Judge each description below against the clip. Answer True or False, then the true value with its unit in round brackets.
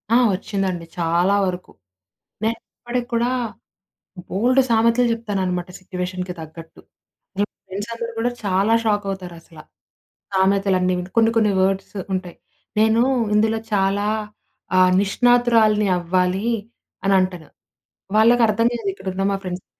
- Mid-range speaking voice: False (195 Hz)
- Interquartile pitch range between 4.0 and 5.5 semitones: False (3.5 semitones)